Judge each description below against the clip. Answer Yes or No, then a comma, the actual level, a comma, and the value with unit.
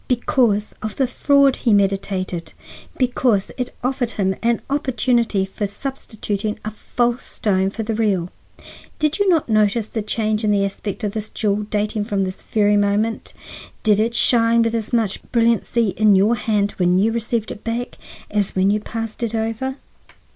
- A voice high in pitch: Yes, high, 220 Hz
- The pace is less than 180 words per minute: Yes, average, 170 wpm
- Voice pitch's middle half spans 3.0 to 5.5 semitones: No, narrow, 2.5 semitones